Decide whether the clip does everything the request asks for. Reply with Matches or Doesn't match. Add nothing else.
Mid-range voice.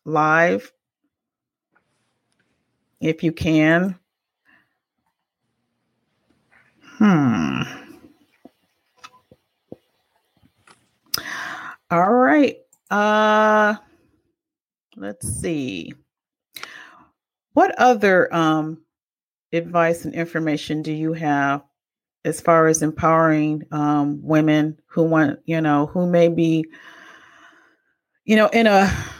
Matches